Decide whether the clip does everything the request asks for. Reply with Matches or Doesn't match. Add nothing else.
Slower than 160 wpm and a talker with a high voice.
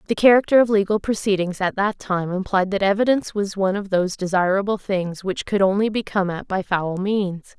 Doesn't match